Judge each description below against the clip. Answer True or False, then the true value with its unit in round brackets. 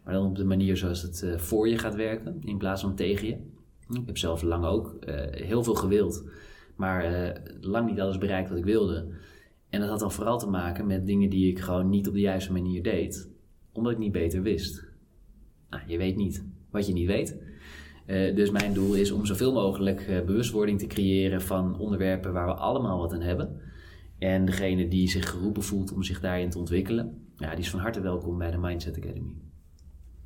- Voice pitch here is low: True (95 Hz)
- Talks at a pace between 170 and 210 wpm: True (200 wpm)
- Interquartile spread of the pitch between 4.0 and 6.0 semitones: False (2.6 semitones)